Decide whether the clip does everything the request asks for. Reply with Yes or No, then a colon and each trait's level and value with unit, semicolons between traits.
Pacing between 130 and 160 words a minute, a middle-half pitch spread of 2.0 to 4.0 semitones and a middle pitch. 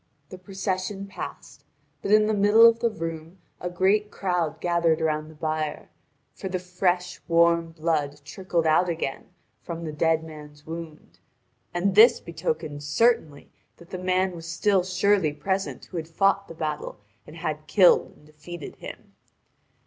Yes: average, 155 wpm; average, 3.3 semitones; medium, 170 Hz